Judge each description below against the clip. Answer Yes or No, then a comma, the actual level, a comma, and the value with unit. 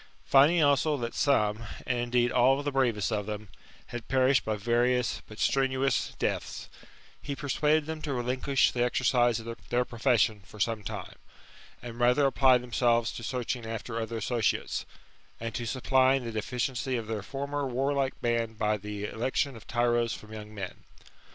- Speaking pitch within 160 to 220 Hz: No, low, 120 Hz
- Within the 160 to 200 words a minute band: Yes, average, 165 wpm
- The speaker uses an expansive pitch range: No, average, 2.9 semitones